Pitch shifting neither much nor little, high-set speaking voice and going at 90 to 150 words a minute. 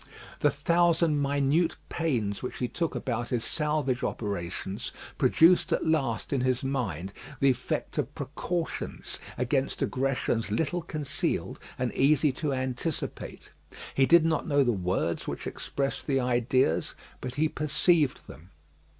No: average, 4.0 semitones; low, 135 Hz; slow, 135 wpm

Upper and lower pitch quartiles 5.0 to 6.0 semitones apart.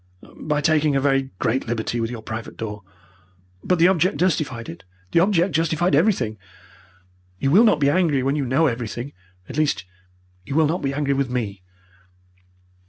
Yes: average, 5.3 semitones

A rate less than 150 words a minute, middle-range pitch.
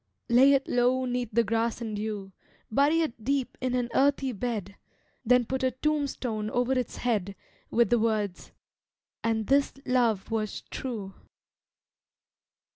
No: average, 140 wpm; high, 240 Hz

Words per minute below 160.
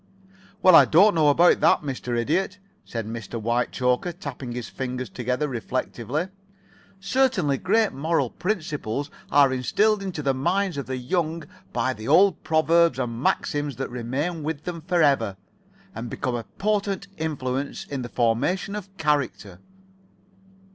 Yes: average, 140 wpm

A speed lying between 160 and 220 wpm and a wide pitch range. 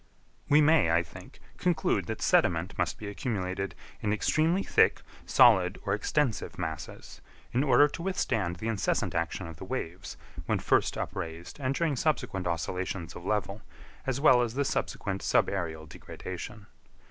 No: average, 150 wpm; wide, 7.0 semitones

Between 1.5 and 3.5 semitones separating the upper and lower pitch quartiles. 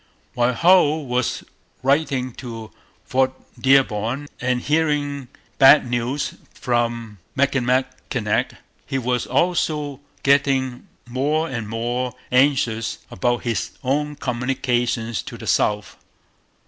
Yes: average, 2.8 semitones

